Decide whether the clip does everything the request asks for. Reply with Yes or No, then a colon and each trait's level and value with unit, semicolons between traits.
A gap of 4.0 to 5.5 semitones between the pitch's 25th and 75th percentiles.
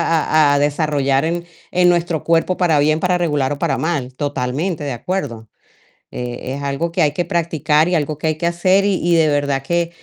No: average, 3.2 semitones